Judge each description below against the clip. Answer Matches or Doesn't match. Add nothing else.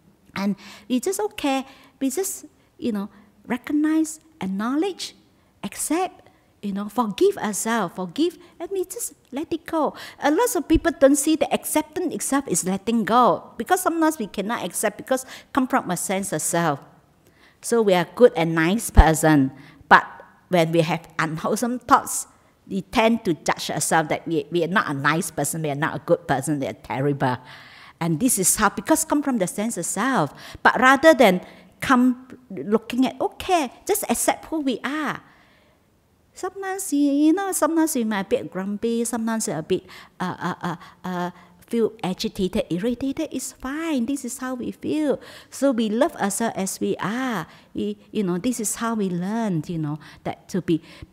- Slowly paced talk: Doesn't match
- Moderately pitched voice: Doesn't match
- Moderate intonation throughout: Doesn't match